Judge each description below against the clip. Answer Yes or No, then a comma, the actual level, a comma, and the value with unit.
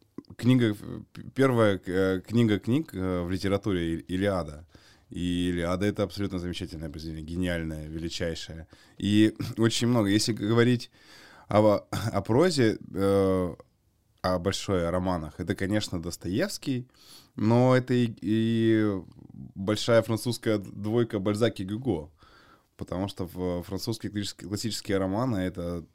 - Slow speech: Yes, slow, 105 wpm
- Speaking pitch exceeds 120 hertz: No, low, 100 Hz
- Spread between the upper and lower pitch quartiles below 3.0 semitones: No, average, 3.8 semitones